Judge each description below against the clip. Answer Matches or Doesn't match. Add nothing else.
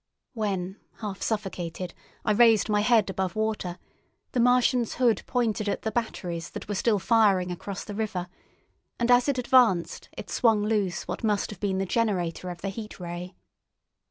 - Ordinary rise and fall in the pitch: Matches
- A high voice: Matches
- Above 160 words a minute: Matches